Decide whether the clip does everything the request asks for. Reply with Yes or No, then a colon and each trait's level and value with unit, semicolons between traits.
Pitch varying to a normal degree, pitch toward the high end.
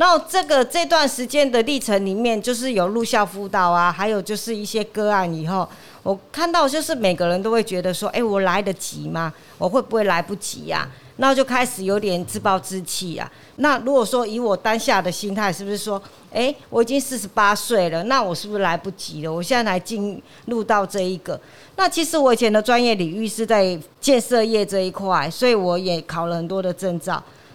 Yes: average, 4.5 semitones; high, 205 Hz